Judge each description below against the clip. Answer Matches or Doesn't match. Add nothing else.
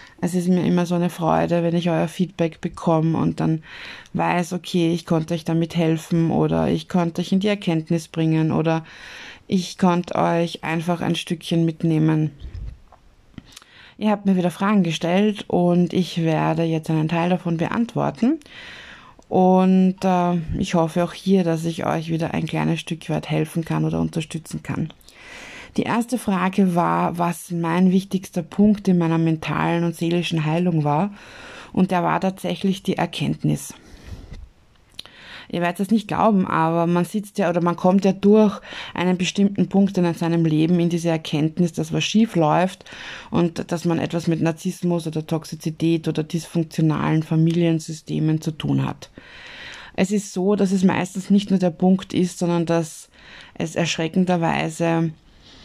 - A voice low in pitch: Doesn't match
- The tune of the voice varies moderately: Doesn't match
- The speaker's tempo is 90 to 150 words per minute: Doesn't match